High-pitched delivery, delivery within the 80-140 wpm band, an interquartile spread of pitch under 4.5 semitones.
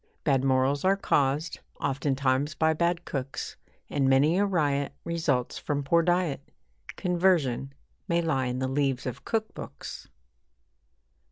No: medium, 145 Hz; slow, 135 wpm; average, 4.0 semitones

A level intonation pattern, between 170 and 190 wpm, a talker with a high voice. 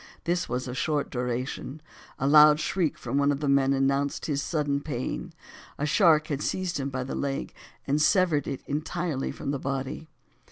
No: narrow, 2.2 semitones; average, 185 wpm; medium, 140 Hz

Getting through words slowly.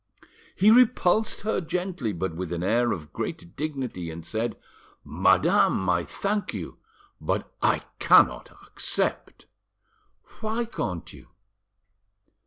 Yes: slow, 115 wpm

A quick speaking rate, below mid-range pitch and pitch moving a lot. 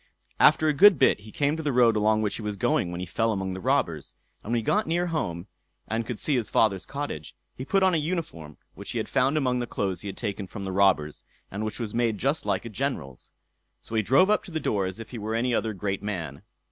Yes: fast, 260 wpm; low, 110 Hz; wide, 5.9 semitones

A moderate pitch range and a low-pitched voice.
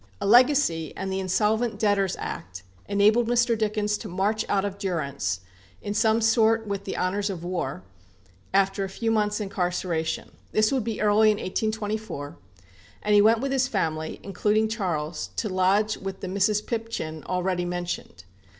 No: average, 3.1 semitones; high, 205 Hz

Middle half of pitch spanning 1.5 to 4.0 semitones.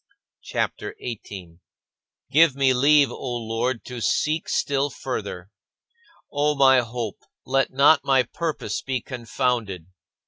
Yes: average, 3.2 semitones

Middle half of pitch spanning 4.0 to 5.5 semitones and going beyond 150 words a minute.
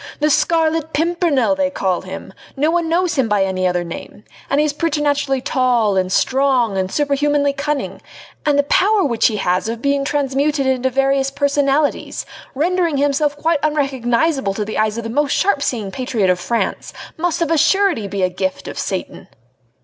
Yes: average, 4.9 semitones; average, 180 wpm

